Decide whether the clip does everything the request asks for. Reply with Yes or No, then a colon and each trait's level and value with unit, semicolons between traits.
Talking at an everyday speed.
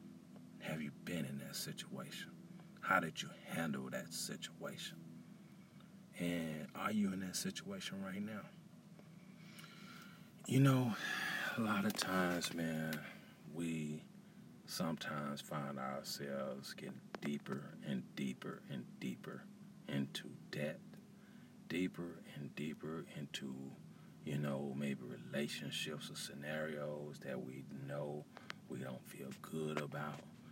No: slow, 110 wpm